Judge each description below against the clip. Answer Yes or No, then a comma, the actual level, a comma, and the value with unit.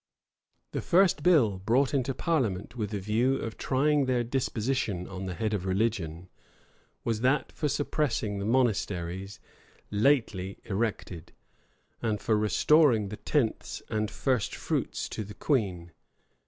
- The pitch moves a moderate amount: Yes, average, 5.0 semitones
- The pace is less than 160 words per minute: Yes, average, 140 wpm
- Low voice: Yes, low, 110 Hz